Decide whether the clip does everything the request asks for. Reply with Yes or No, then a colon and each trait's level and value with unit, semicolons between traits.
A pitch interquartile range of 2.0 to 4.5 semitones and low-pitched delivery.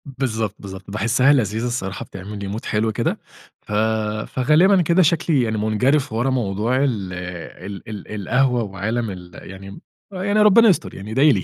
No: average, 5.3 semitones; low, 110 Hz